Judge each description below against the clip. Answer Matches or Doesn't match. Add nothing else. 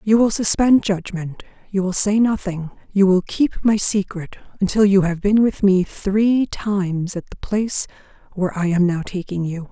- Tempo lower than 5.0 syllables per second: Matches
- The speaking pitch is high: Matches